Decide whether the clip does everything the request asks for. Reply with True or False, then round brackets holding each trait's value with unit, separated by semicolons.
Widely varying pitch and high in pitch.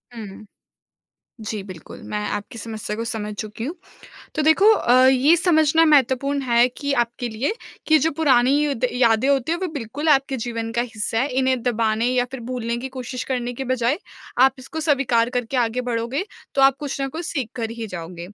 False (3.4 semitones; 250 Hz)